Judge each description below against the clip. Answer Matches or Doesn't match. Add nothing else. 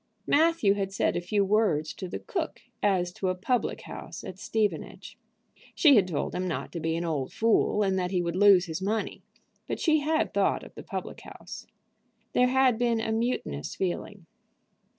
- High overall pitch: Matches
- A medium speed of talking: Matches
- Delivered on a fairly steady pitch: Doesn't match